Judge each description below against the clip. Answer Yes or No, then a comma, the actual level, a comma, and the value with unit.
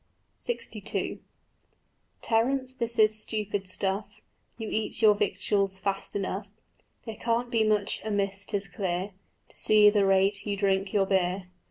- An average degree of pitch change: No, narrow, 2.0 semitones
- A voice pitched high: Yes, high, 205 Hz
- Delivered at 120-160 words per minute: Yes, average, 140 wpm